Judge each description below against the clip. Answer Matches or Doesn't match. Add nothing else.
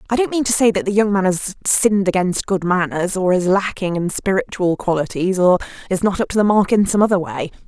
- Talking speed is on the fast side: Matches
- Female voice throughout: Matches